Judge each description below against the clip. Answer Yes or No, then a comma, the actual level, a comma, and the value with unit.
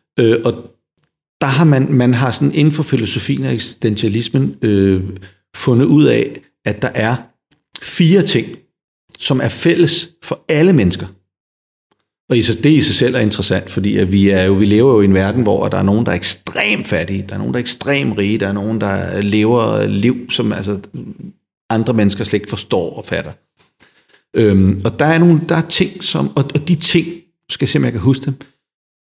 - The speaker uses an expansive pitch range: Yes, wide, 6.2 semitones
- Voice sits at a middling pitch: No, low, 120 Hz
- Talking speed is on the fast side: No, average, 195 wpm